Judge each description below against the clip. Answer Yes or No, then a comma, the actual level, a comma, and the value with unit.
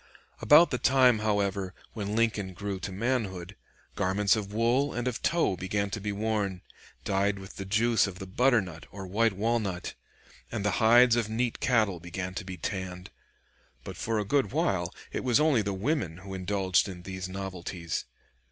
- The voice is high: No, low, 100 Hz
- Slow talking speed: No, average, 175 wpm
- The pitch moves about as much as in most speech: Yes, average, 3.4 semitones